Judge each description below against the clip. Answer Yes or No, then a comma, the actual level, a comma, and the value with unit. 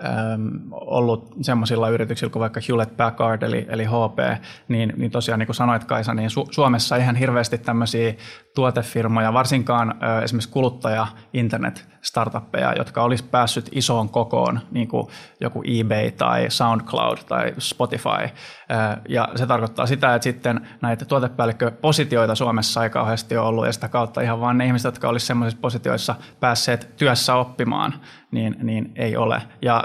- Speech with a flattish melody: Yes, narrow, 1.5 semitones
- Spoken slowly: No, average, 150 wpm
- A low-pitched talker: Yes, low, 115 Hz